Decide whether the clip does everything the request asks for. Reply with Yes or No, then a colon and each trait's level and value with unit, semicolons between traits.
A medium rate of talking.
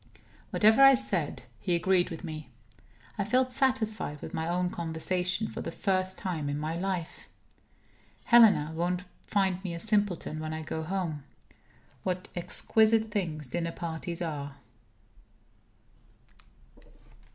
No: slow, 130 wpm